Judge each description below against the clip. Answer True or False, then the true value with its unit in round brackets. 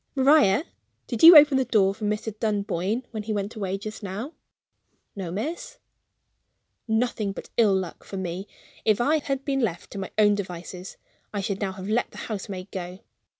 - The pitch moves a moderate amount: True (3.9 semitones)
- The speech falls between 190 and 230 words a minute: False (180 wpm)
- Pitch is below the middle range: False (210 Hz)